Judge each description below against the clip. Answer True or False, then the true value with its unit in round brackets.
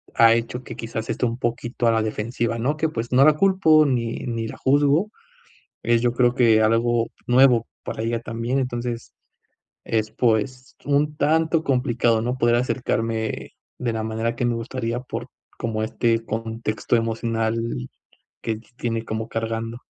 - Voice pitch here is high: False (115 Hz)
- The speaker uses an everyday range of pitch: False (1.9 semitones)